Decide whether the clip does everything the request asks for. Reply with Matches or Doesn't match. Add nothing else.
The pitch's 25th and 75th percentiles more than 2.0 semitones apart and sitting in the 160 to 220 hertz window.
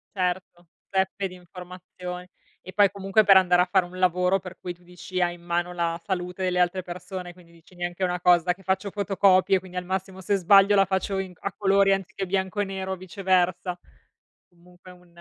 Doesn't match